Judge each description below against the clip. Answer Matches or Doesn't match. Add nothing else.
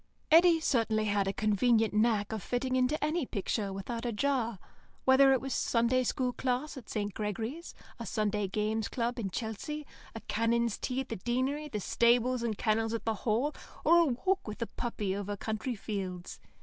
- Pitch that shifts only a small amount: Doesn't match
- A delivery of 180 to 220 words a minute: Matches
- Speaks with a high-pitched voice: Matches